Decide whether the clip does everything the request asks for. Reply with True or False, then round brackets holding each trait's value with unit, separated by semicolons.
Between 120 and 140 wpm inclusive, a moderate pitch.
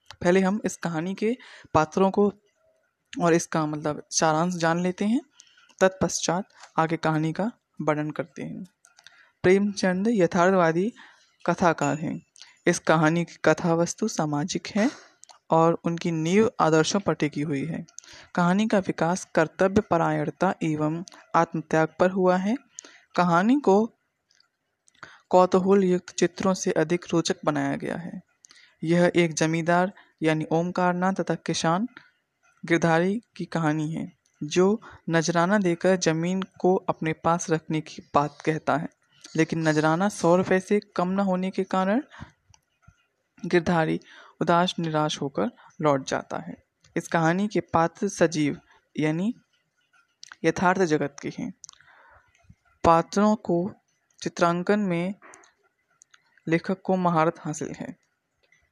True (125 wpm; 175 Hz)